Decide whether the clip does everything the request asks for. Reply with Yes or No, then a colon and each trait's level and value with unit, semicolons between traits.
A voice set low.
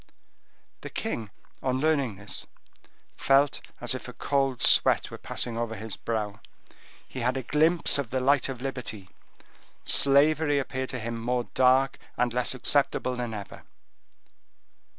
Yes: low, 130 Hz